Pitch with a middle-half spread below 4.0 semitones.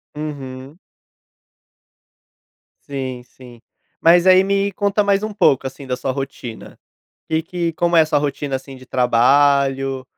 No: average, 4.6 semitones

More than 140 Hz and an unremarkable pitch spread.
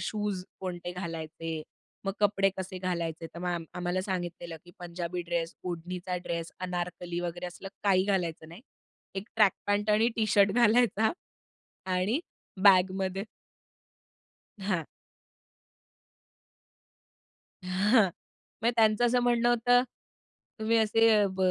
Yes: medium, 185 Hz; average, 3.0 semitones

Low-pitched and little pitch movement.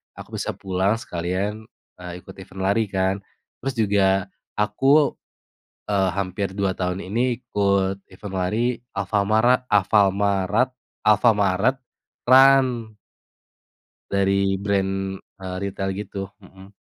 Yes: low, 100 Hz; narrow, 2.2 semitones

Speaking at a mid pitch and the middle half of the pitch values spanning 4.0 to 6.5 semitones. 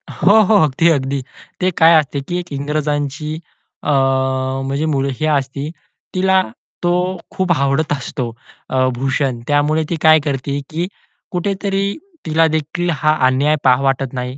No: medium, 150 Hz; average, 3.4 semitones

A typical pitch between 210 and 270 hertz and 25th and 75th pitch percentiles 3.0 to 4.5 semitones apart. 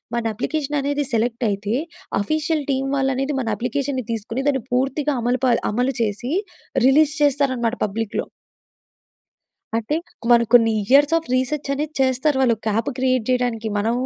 Yes: very high, 255 Hz; average, 3.5 semitones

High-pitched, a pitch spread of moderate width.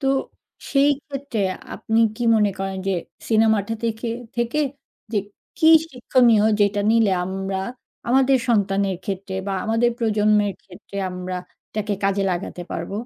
Yes: high, 215 Hz; average, 3.3 semitones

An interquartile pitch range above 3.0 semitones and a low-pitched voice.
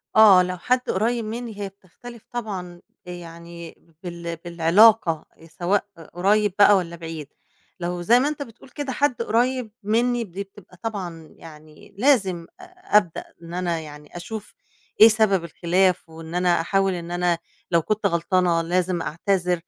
No: average, 4.2 semitones; medium, 180 Hz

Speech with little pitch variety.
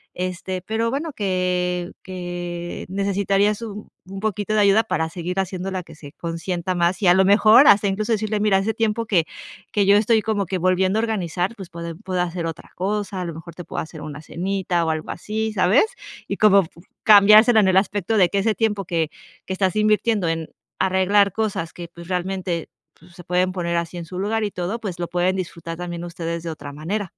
No: average, 3.0 semitones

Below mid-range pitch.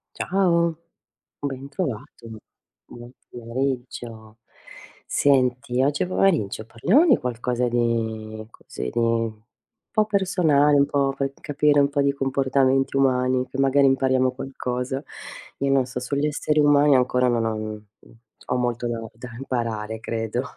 Yes: low, 130 Hz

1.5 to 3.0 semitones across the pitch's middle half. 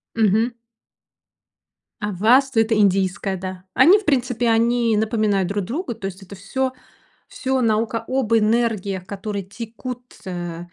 No: average, 3.5 semitones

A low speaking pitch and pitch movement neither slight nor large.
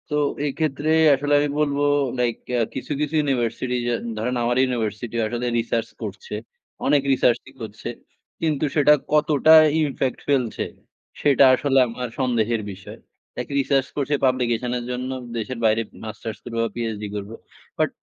Yes: low, 125 Hz; average, 3.6 semitones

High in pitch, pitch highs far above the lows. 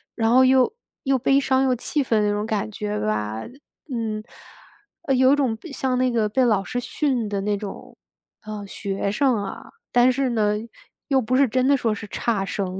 No: high, 230 Hz; average, 3.9 semitones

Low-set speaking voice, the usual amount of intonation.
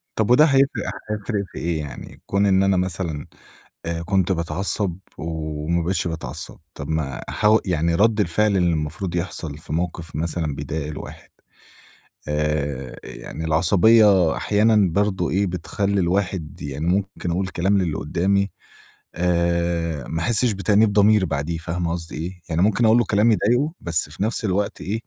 Yes: very low, 90 Hz; average, 3.8 semitones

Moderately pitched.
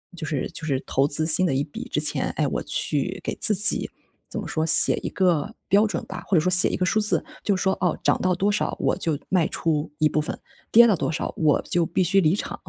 Yes: medium, 170 Hz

